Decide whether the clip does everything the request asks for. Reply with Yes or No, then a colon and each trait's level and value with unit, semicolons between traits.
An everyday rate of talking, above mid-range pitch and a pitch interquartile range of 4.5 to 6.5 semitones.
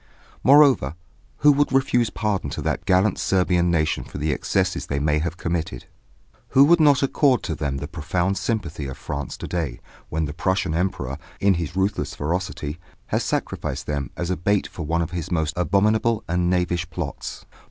No: average, 180 wpm; very low, 90 Hz; average, 4.8 semitones